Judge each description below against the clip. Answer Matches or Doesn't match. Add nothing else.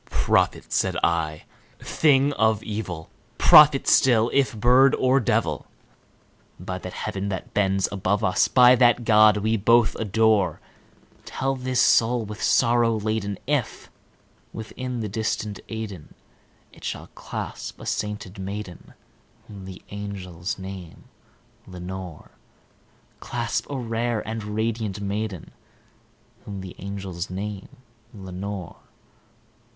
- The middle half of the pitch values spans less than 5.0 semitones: Matches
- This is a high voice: Doesn't match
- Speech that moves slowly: Matches